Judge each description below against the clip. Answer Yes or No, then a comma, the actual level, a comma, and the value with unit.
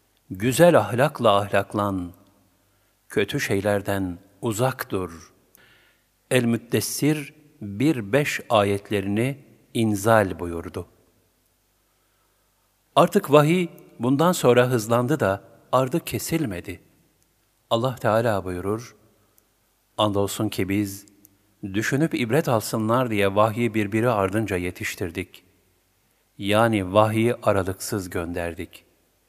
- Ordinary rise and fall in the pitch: Yes, average, 3.9 semitones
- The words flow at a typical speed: No, slow, 80 wpm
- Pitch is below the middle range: Yes, low, 110 Hz